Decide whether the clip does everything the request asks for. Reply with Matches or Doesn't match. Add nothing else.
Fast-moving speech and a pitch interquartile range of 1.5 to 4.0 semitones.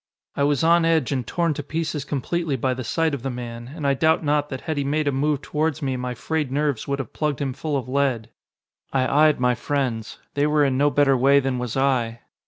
Matches